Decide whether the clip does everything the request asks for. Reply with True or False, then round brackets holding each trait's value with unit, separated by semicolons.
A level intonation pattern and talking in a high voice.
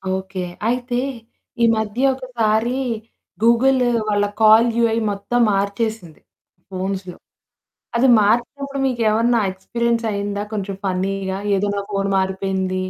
False (3.5 semitones; 215 Hz)